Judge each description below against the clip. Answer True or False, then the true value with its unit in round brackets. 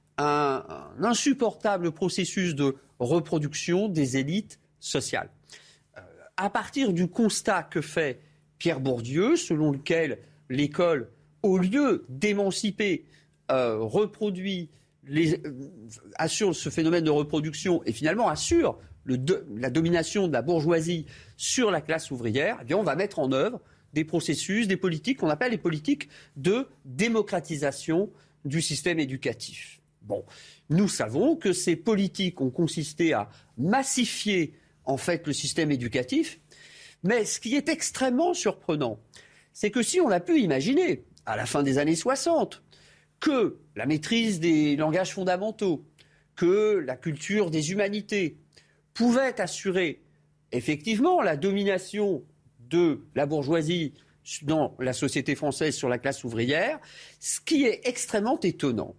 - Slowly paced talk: True (135 wpm)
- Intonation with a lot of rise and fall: True (5.9 semitones)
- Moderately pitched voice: True (170 Hz)